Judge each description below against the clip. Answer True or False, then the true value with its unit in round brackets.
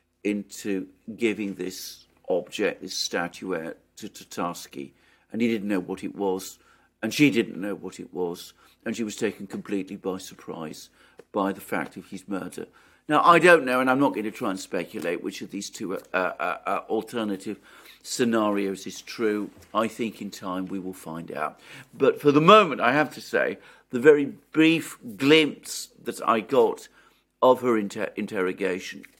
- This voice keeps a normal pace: True (175 wpm)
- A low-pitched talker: True (105 Hz)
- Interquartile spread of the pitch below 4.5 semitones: False (5.0 semitones)